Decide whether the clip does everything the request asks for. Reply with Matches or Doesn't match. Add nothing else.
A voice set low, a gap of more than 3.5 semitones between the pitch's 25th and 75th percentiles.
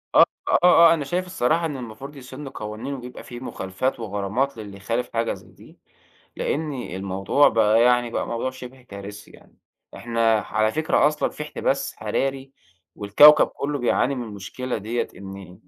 Matches